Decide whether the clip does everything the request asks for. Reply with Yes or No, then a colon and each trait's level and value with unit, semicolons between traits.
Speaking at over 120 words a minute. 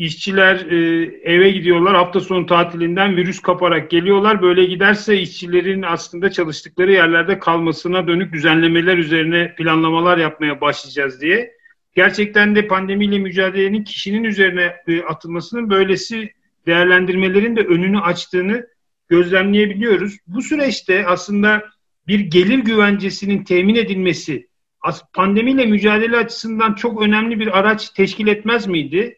No: average, 110 wpm